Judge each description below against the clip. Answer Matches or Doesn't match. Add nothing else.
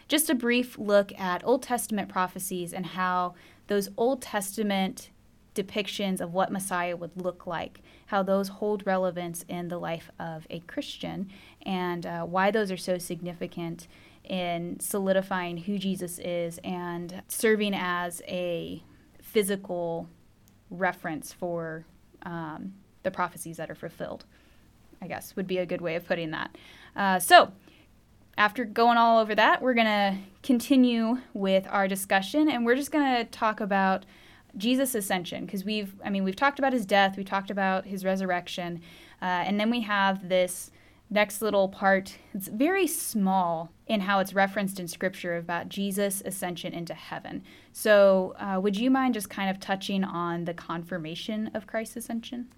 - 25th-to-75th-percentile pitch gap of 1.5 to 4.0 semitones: Matches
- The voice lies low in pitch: Doesn't match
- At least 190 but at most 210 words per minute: Doesn't match